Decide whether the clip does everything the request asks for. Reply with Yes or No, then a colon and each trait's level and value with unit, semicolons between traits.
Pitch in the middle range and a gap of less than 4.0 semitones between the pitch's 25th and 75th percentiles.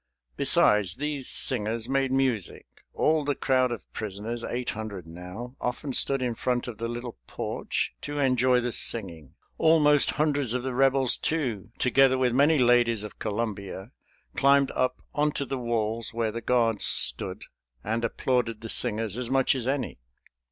No: low, 120 Hz; average, 3.2 semitones